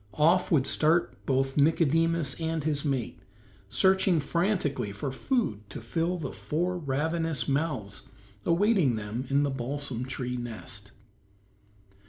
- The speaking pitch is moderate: Yes, medium, 145 Hz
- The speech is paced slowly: Yes, slow, 130 wpm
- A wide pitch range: No, average, 4.5 semitones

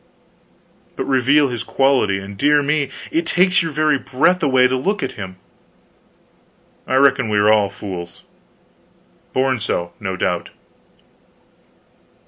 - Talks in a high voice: No, low, 130 Hz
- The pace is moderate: No, slow, 130 wpm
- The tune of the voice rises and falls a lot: Yes, wide, 6.3 semitones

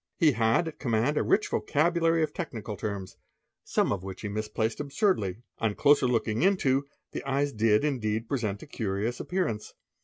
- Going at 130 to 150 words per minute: No, average, 165 wpm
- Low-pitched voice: Yes, low, 120 Hz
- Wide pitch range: Yes, wide, 5.7 semitones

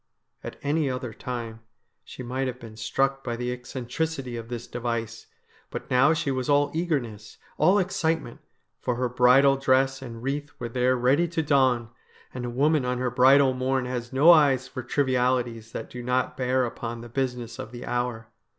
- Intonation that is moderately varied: No, narrow, 2.1 semitones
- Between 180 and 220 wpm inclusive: Yes, average, 185 wpm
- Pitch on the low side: Yes, low, 125 Hz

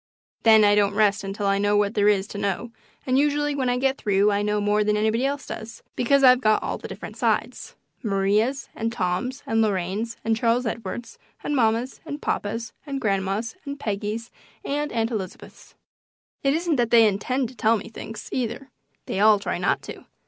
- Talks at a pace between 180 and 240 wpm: Yes, average, 195 wpm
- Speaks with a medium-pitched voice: No, high, 225 Hz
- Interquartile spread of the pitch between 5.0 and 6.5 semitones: No, average, 3.6 semitones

